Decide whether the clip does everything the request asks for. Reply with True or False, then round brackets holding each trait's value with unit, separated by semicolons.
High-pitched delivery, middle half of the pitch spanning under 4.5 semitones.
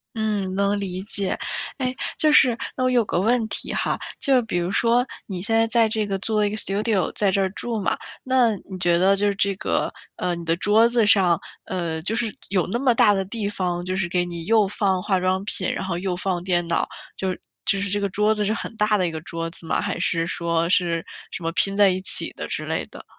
True (195 Hz; 3.3 semitones)